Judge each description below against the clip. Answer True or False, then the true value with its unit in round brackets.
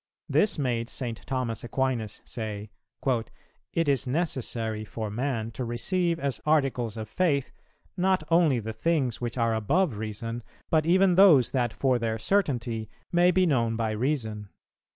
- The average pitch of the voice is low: True (125 Hz)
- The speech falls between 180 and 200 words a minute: False (150 wpm)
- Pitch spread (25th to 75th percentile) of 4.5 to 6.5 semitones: True (5.6 semitones)